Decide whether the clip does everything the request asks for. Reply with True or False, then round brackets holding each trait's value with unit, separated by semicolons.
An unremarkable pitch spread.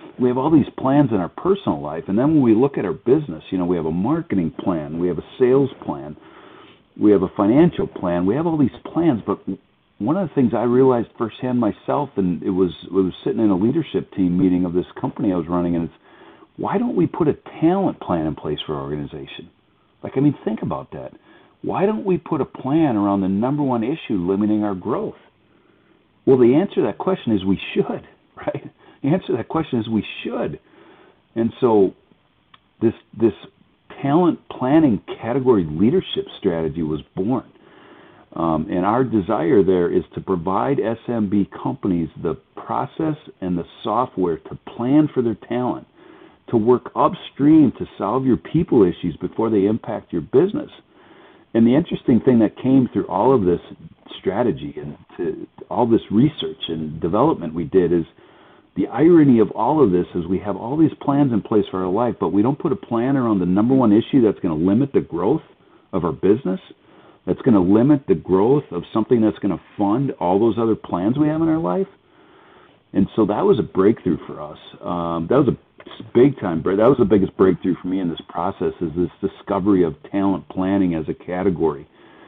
False (6.3 semitones)